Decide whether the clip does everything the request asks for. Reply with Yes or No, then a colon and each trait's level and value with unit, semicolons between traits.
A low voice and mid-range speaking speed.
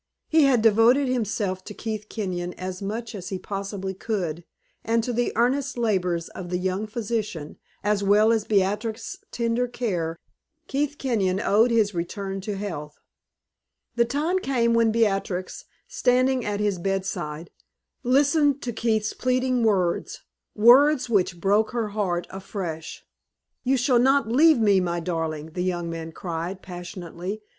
No: high, 210 Hz; average, 145 wpm